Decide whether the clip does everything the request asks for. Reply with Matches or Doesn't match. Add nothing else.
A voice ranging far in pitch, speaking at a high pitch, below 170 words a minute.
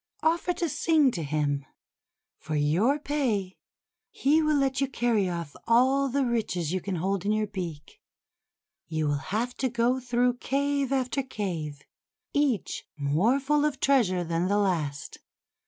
Matches